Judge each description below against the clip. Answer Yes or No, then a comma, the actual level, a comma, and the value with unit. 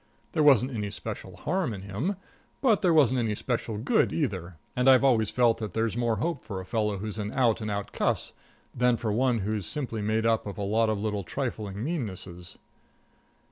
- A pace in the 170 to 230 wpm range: Yes, average, 200 wpm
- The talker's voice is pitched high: No, low, 110 Hz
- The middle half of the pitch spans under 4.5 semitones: Yes, average, 3.6 semitones